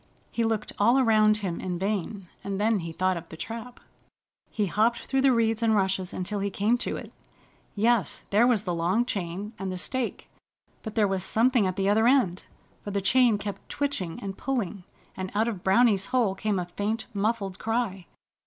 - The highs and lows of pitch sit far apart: No, average, 3.3 semitones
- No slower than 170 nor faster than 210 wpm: Yes, average, 195 wpm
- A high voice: Yes, high, 205 Hz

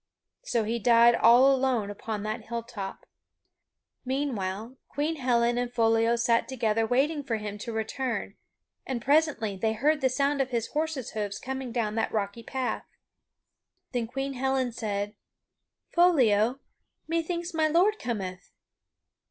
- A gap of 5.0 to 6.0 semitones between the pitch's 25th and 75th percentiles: No, average, 3.5 semitones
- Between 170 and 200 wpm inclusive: No, slow, 135 wpm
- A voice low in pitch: No, high, 240 Hz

